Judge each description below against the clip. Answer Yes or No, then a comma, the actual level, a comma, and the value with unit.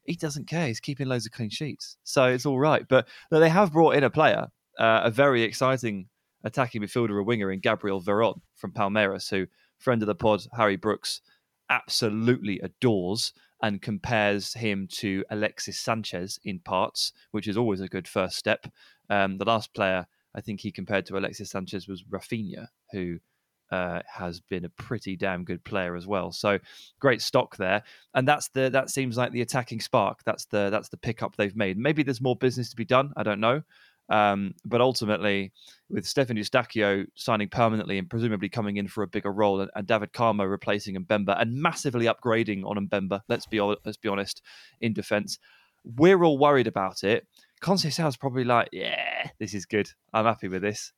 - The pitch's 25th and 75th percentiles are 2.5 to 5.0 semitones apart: Yes, average, 3.8 semitones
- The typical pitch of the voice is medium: No, low, 110 Hz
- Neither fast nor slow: Yes, average, 190 wpm